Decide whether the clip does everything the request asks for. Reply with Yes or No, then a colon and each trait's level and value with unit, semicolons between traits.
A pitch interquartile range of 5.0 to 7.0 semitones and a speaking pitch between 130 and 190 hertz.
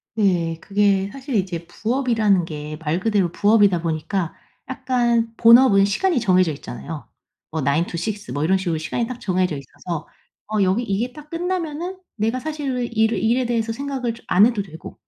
No: wide, 5.6 semitones; high, 210 Hz